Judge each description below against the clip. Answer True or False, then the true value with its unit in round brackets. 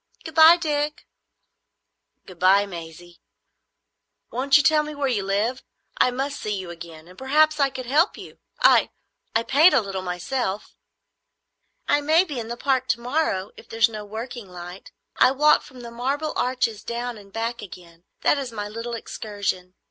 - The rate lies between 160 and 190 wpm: True (175 wpm)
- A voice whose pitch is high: True (235 Hz)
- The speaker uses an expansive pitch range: True (6.1 semitones)